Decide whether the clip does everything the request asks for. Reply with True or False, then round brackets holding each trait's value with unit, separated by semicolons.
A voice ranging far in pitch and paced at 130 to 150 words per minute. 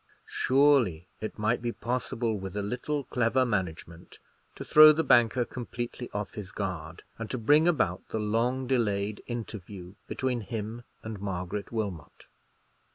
False (3.9 semitones; 145 wpm)